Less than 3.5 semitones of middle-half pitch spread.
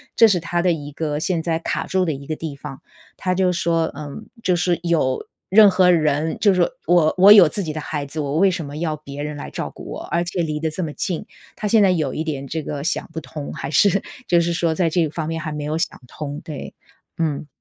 Yes: average, 2.8 semitones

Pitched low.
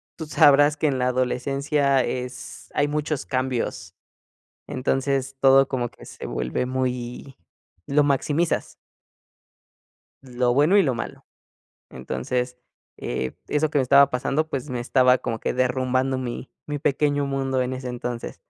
Yes: low, 130 Hz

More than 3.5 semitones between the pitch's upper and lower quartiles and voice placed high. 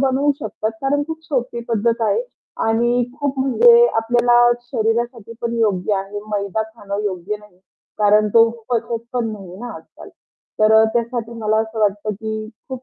No: narrow, 2.4 semitones; high, 225 Hz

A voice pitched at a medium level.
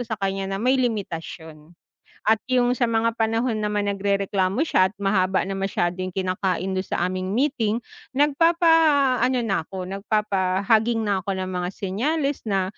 No: high, 205 Hz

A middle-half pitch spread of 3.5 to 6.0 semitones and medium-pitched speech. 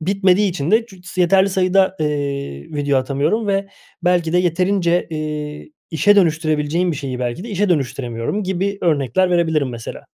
Yes: average, 4.6 semitones; medium, 170 Hz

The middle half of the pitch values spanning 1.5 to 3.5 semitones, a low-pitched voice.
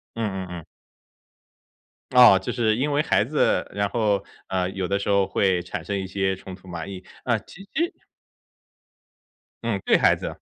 Yes: average, 2.8 semitones; low, 100 Hz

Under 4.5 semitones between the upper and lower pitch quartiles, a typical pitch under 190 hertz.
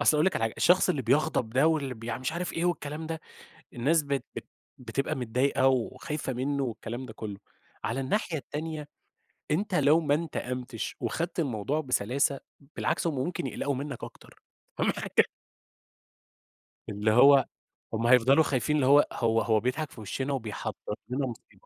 Yes: average, 3.8 semitones; low, 135 Hz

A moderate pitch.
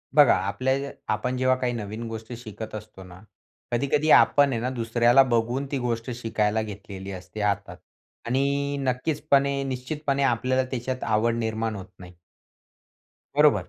No: low, 120 Hz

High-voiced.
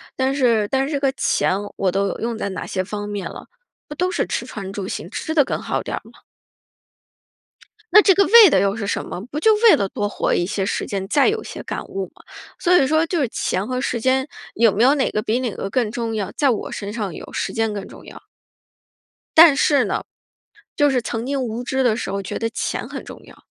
Yes: high, 235 Hz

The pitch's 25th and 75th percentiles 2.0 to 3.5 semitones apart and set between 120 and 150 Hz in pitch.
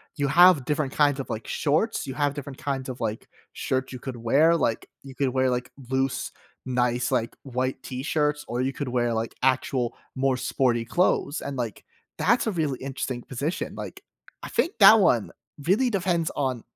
Yes: average, 3.0 semitones; low, 135 Hz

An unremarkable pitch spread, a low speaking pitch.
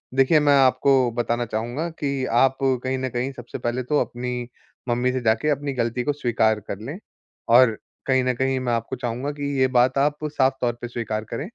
No: narrow, 2.3 semitones; low, 130 Hz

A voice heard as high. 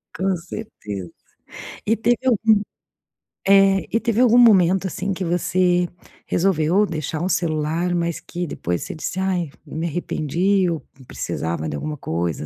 No: medium, 175 Hz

